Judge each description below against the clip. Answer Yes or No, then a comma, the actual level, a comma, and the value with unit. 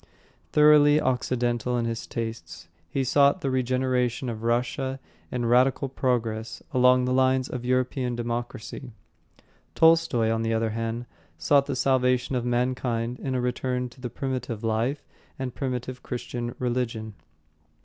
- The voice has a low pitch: Yes, low, 125 Hz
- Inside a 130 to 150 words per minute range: Yes, average, 140 wpm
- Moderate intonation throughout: No, narrow, 1.8 semitones